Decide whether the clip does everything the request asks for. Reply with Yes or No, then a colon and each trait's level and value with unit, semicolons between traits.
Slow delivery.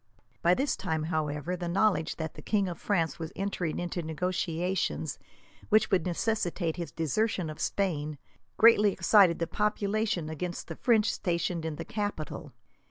No: average, 155 wpm